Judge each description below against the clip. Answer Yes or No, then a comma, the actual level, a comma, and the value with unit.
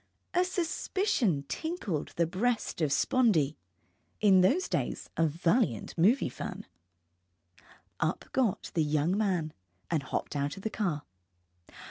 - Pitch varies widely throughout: Yes, wide, 7.9 semitones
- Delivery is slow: Yes, slow, 130 wpm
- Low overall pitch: No, medium, 185 Hz